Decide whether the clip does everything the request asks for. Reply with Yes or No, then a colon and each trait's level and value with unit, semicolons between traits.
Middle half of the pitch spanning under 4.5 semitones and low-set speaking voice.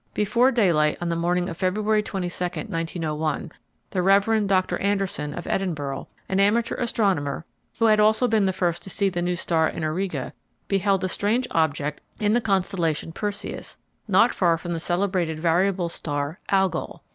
No: average, 3.5 semitones; medium, 185 Hz